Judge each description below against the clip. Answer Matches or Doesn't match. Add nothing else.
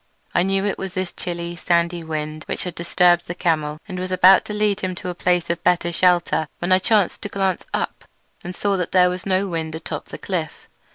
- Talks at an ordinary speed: Doesn't match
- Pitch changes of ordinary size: Doesn't match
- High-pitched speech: Doesn't match